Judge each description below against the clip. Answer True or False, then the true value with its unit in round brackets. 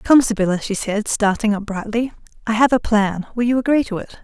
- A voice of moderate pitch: False (220 Hz)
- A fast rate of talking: True (215 wpm)